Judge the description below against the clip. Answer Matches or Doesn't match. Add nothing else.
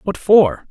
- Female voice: Doesn't match